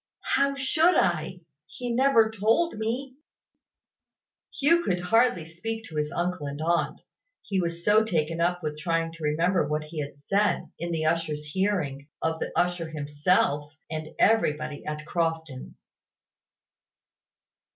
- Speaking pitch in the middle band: Yes, medium, 170 Hz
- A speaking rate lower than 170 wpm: Yes, average, 140 wpm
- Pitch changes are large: Yes, wide, 5.9 semitones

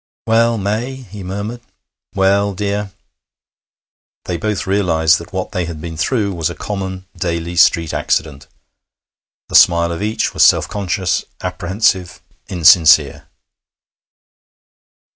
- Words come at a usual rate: No, slow, 120 wpm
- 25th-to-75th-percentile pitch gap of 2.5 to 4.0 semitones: Yes, average, 3.3 semitones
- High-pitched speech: No, very low, 95 Hz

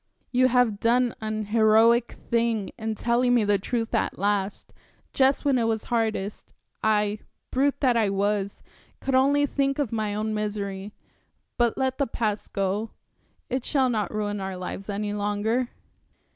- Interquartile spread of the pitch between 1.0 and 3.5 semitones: Yes, average, 3.0 semitones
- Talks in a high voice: Yes, high, 220 Hz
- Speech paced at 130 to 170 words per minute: Yes, average, 160 wpm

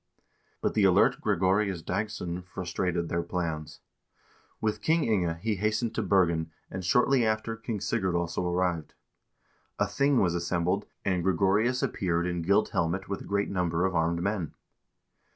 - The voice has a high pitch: No, very low, 95 Hz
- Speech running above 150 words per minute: Yes, average, 160 wpm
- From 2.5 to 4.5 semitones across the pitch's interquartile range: Yes, average, 3.5 semitones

